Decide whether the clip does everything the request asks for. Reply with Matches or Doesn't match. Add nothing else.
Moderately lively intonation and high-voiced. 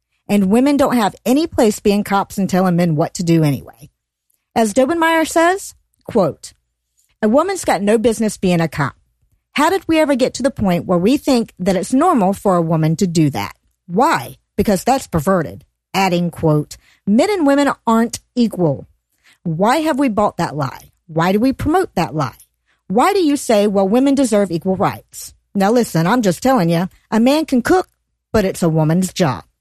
Doesn't match